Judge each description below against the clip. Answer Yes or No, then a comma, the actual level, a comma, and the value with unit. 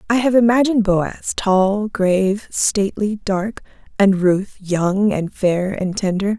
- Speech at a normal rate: No, slow, 120 wpm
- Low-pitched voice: No, high, 200 Hz